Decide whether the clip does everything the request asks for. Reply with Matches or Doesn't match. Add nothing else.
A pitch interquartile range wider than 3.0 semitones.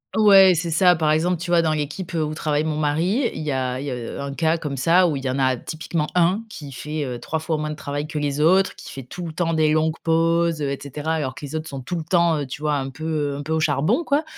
Doesn't match